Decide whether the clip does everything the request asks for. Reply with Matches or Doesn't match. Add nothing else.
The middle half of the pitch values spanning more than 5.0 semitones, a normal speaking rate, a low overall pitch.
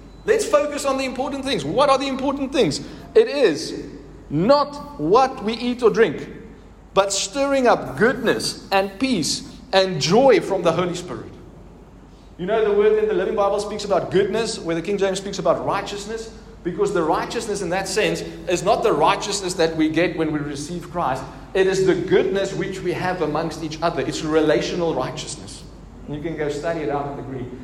Doesn't match